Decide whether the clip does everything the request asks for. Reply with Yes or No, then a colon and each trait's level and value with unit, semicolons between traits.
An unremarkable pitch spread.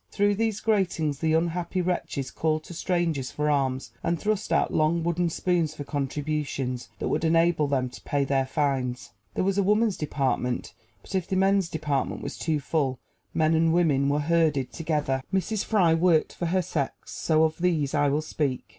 Yes: average, 3.6 semitones